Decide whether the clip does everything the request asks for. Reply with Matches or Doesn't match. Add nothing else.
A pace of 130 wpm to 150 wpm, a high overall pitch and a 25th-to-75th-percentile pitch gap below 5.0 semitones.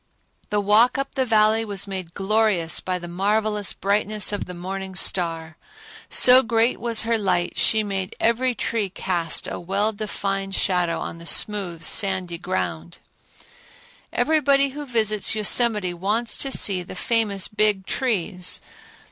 Matches